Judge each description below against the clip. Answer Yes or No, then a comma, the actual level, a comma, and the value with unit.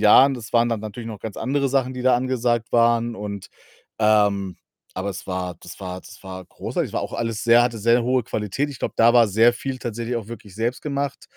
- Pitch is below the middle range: Yes, low, 115 Hz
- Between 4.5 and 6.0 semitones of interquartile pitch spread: No, average, 2.9 semitones